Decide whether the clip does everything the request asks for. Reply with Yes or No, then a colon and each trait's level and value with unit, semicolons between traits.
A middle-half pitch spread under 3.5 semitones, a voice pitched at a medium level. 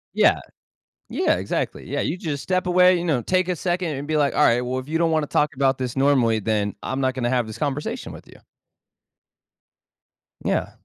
No: average, 4.8 semitones; medium, 145 Hz